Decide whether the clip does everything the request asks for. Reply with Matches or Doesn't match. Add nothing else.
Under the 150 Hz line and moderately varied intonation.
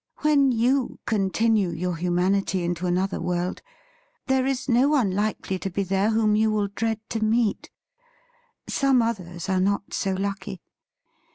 Doesn't match